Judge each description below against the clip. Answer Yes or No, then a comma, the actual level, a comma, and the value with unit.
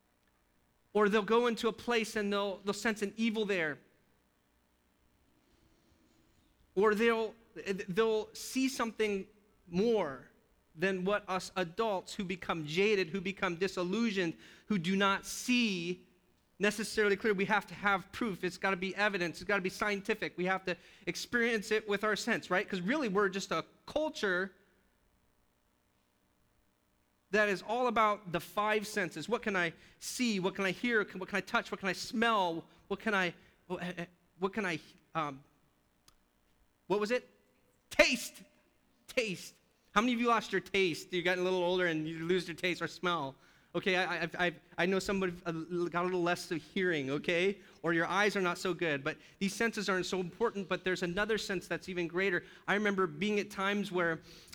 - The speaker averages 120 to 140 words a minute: No, average, 175 wpm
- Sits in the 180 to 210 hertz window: Yes, high, 190 Hz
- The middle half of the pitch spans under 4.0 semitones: Yes, average, 3.4 semitones